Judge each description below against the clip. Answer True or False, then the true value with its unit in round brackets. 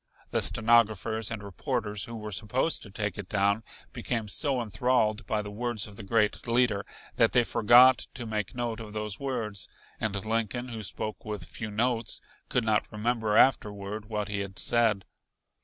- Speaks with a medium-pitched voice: False (110 Hz)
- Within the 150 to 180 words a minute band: True (175 wpm)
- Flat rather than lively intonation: True (2.2 semitones)